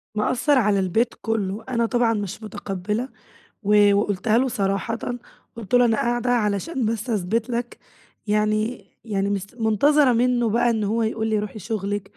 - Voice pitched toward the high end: Yes, high, 220 Hz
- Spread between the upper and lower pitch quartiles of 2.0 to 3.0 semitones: Yes, average, 2.7 semitones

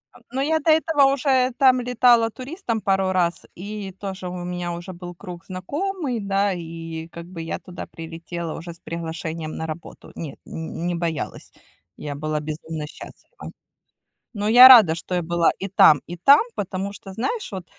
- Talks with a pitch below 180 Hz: No, medium, 185 Hz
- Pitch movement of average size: No, wide, 5.8 semitones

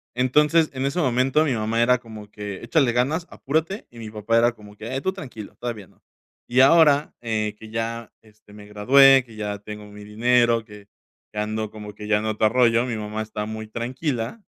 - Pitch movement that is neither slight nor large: Yes, average, 3.5 semitones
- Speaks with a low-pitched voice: Yes, low, 115 Hz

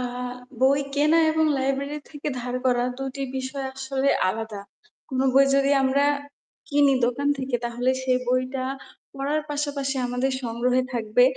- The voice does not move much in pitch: Yes, narrow, 1.9 semitones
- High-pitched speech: Yes, very high, 265 Hz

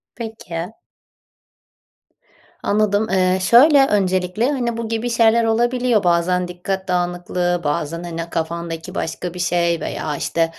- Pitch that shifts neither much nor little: Yes, average, 4.6 semitones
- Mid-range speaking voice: Yes, medium, 180 Hz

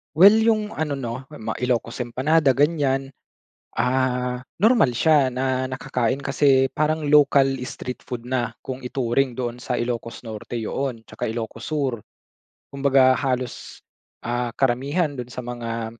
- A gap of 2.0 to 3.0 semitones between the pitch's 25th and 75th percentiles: Yes, narrow, 2.5 semitones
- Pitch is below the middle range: Yes, low, 130 Hz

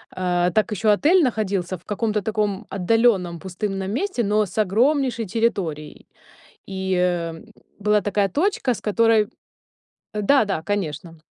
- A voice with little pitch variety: No, average, 3.7 semitones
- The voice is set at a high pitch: Yes, high, 205 Hz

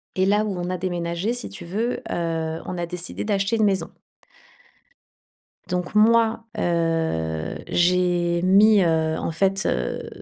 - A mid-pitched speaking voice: Yes, medium, 180 Hz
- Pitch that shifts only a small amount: No, average, 3.1 semitones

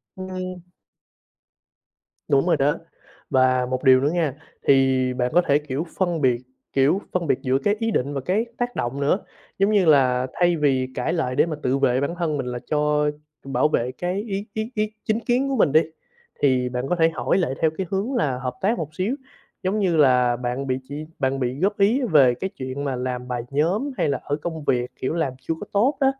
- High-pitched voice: No, medium, 150 Hz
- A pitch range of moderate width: No, wide, 6.3 semitones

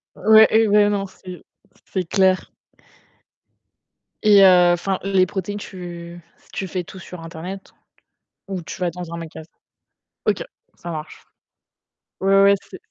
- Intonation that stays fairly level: Yes, narrow, 2.1 semitones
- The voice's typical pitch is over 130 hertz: Yes, medium, 185 Hz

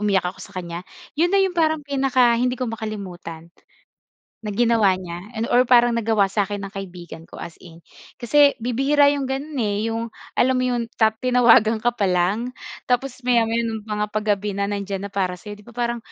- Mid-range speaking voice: No, high, 225 Hz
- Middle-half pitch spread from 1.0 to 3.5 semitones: No, average, 3.9 semitones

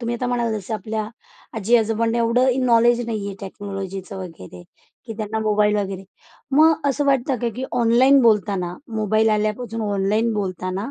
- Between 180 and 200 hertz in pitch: No, high, 220 Hz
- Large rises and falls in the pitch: No, average, 3.0 semitones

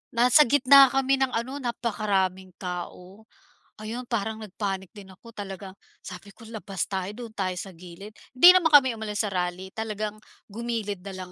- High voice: Yes, high, 210 Hz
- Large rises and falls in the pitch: No, average, 3.8 semitones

